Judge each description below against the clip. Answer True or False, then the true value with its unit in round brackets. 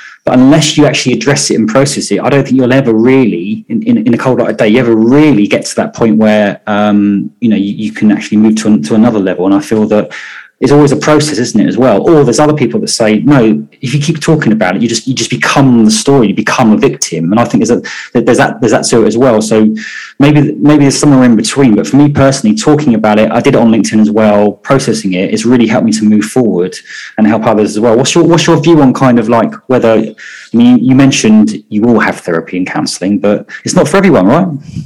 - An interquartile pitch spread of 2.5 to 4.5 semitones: False (5.2 semitones)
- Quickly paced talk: True (265 wpm)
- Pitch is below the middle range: True (120 Hz)